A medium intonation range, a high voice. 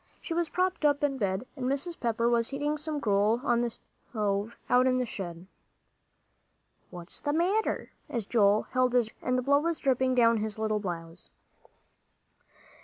Yes: average, 5.0 semitones; high, 245 Hz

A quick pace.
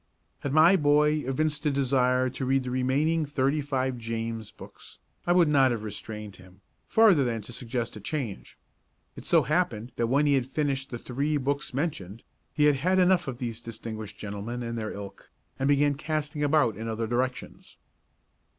No: average, 180 wpm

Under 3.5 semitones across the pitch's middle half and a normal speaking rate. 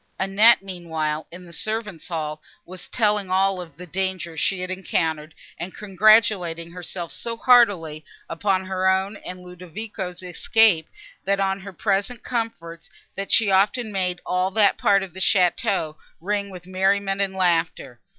Yes: narrow, 2.6 semitones; average, 150 wpm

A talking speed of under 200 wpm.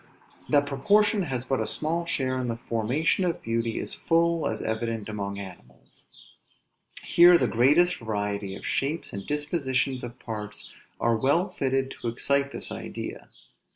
Yes: average, 155 wpm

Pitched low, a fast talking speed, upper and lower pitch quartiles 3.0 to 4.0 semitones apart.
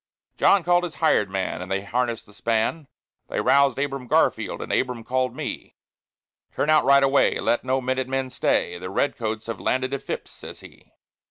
No: low, 130 Hz; average, 190 wpm; average, 3.4 semitones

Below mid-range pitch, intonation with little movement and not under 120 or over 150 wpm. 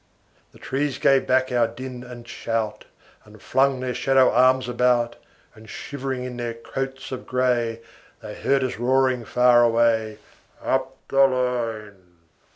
Yes: low, 125 Hz; narrow, 2.0 semitones; average, 145 wpm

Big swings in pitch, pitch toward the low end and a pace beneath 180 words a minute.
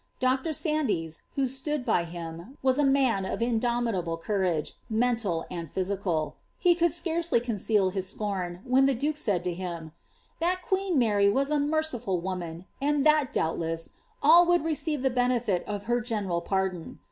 No: wide, 7.5 semitones; high, 230 Hz; average, 160 wpm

